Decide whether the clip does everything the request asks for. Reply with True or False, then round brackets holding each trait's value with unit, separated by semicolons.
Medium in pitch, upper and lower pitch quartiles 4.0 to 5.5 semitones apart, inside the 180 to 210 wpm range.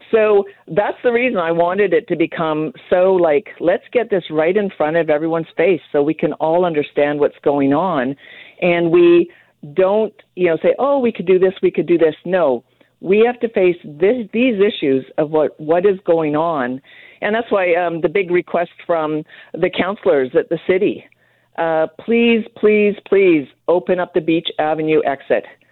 True (175 Hz; 4.4 semitones; 185 wpm)